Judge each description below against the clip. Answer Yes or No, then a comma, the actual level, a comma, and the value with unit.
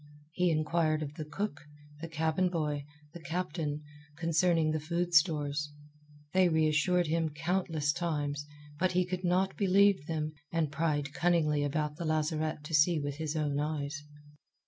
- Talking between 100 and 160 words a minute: Yes, average, 150 wpm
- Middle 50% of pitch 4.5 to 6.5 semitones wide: No, narrow, 2.5 semitones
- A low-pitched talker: No, medium, 155 Hz